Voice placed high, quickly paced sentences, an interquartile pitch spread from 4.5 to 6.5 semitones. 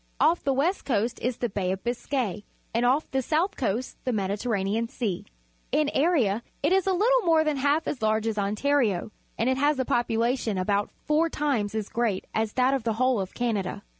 Yes: high, 240 Hz; fast, 210 wpm; average, 5.2 semitones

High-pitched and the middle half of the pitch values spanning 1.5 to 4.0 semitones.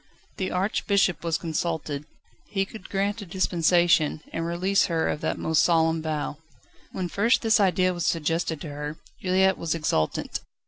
No: medium, 170 Hz; average, 3.0 semitones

